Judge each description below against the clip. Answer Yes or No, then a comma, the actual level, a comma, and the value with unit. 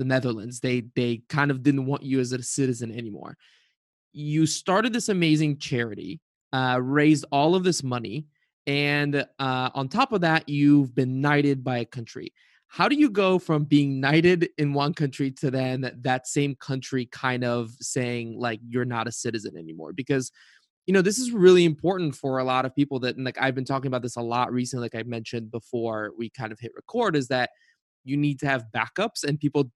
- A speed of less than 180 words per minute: No, fast, 205 wpm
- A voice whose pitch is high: No, low, 135 Hz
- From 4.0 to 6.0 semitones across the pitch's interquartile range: No, average, 3.1 semitones